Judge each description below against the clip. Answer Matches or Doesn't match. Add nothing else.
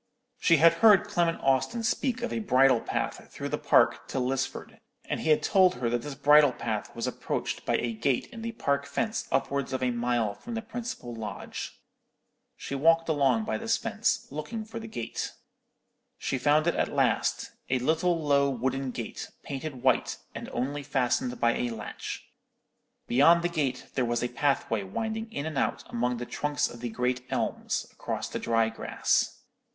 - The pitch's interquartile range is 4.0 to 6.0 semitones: Matches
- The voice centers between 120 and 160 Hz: Matches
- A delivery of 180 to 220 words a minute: Matches